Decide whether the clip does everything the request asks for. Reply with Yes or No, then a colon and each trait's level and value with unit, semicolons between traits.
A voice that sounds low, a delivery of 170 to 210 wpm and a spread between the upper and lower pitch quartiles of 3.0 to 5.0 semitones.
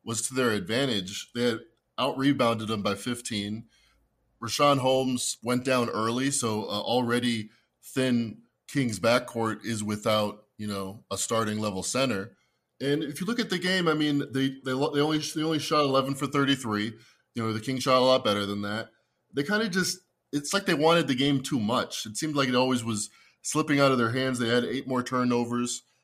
Yes: low, 125 Hz; average, 200 wpm; average, 4.0 semitones